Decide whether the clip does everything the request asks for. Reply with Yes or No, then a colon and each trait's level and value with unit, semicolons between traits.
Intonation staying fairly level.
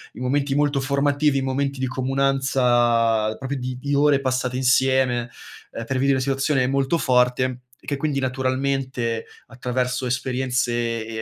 Yes: narrow, 1.6 semitones